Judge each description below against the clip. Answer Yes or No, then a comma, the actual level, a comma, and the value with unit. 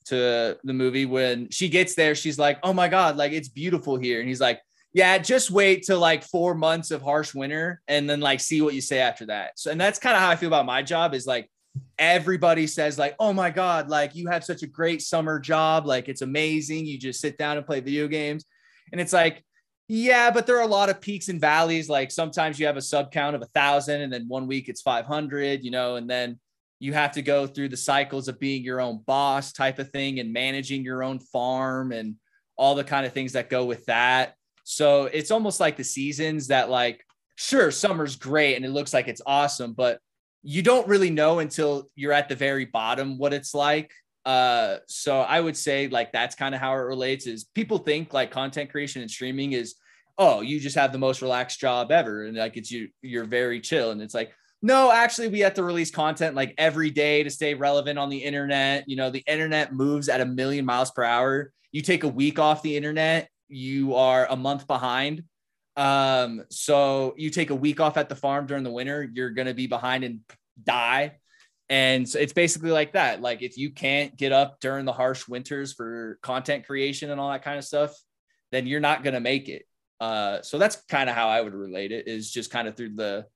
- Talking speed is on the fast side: Yes, fast, 225 wpm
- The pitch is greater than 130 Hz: Yes, medium, 140 Hz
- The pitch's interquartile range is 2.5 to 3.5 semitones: Yes, average, 3.1 semitones